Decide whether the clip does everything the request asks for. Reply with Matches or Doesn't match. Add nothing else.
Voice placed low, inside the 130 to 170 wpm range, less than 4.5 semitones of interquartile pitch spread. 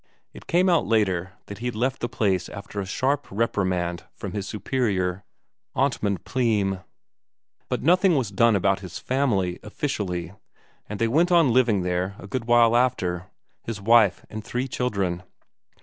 Doesn't match